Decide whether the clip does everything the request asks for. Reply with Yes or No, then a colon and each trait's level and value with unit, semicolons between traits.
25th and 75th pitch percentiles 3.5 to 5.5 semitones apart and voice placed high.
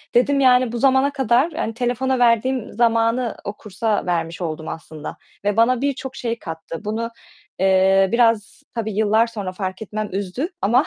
Yes: average, 4.5 semitones; high, 230 Hz